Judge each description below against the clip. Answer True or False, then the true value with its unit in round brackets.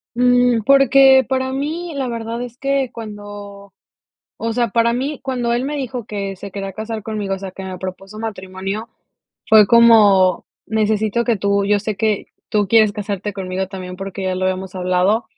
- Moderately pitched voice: False (215 Hz)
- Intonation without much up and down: False (3.6 semitones)